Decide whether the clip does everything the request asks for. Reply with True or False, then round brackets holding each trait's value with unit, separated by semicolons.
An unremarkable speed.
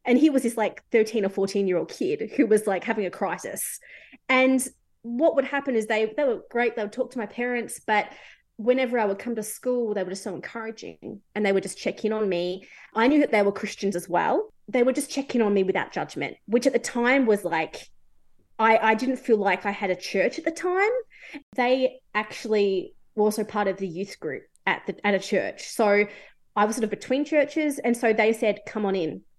False (235 wpm)